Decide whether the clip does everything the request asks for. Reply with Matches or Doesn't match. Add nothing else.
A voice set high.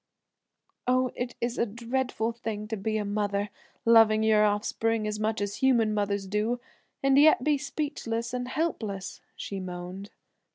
Matches